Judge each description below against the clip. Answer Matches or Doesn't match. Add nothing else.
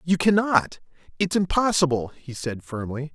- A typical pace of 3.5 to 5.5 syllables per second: Matches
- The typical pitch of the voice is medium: Matches